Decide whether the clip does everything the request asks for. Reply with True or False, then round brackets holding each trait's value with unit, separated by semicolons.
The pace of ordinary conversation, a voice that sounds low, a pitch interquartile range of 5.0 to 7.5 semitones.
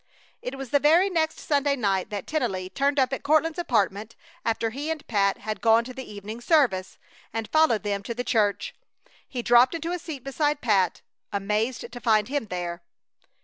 False (190 wpm; 240 Hz; 5.6 semitones)